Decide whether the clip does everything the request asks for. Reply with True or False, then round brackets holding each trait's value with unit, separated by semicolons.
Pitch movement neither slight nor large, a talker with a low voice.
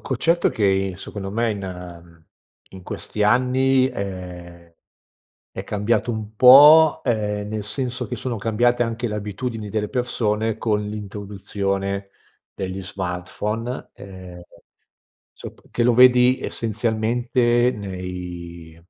True (3.9 semitones; 105 Hz)